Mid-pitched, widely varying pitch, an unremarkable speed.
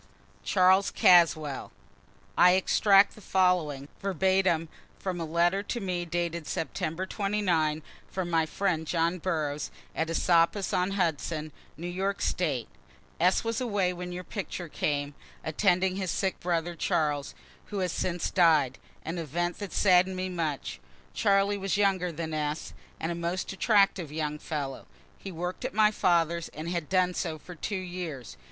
No: medium, 175 Hz; average, 2.8 semitones; average, 155 wpm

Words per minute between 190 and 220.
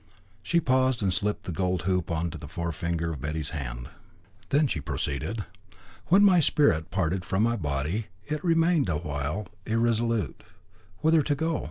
No: average, 165 wpm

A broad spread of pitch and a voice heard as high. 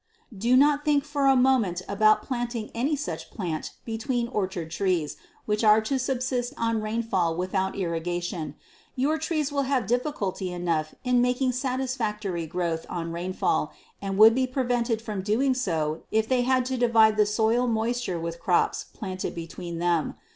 Yes: wide, 5.8 semitones; high, 220 Hz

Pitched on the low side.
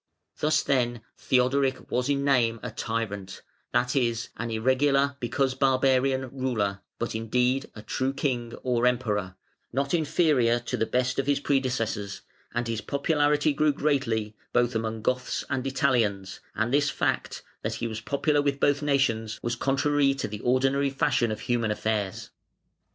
Yes: low, 125 Hz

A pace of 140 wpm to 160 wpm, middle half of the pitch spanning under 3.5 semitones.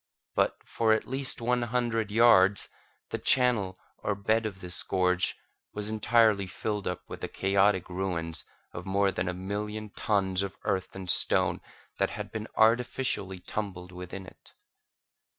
Yes: average, 150 wpm; average, 3.0 semitones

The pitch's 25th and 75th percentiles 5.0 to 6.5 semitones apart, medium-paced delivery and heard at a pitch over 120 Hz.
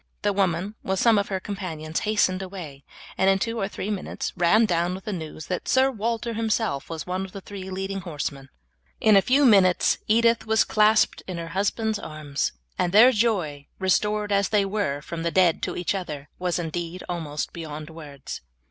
No: average, 4.1 semitones; average, 190 wpm; high, 190 Hz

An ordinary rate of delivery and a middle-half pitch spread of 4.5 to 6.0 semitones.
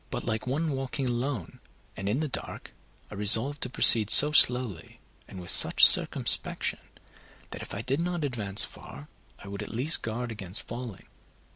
Yes: average, 170 wpm; average, 4.8 semitones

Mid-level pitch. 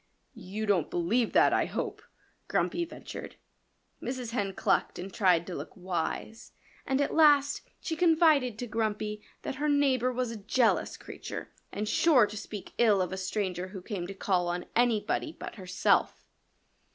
No: high, 215 Hz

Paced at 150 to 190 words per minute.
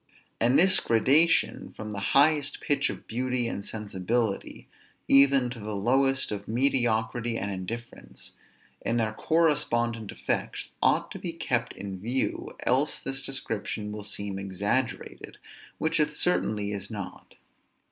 No: slow, 135 wpm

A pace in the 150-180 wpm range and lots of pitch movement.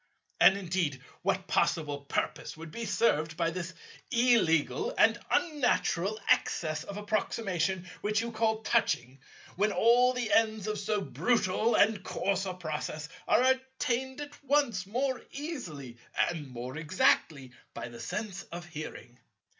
No: average, 140 wpm; wide, 6.4 semitones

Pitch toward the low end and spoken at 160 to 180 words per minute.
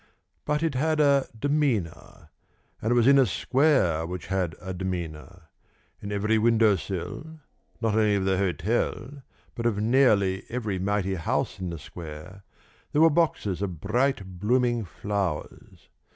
No: low, 105 Hz; average, 150 wpm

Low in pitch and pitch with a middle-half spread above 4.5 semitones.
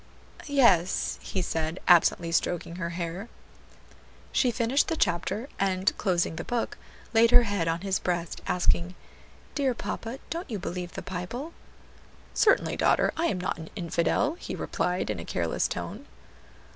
No: medium, 185 Hz; wide, 5.5 semitones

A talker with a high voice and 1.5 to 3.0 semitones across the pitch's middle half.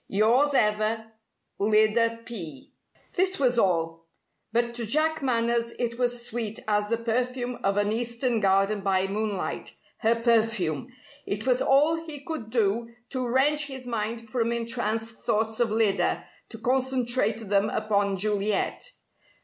Yes: high, 230 Hz; narrow, 2.6 semitones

